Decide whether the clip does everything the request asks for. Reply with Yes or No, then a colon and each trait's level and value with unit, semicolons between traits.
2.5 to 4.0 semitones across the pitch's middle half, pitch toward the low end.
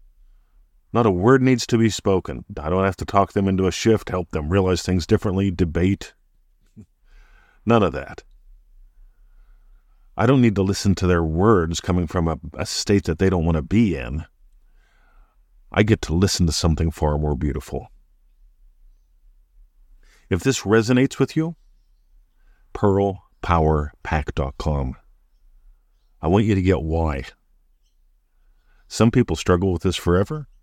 No: average, 4.6 semitones; very low, 90 Hz